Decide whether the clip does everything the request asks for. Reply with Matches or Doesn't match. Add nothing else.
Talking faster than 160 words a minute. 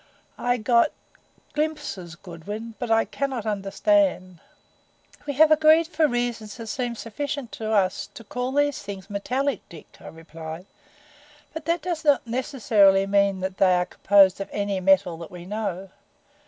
Doesn't match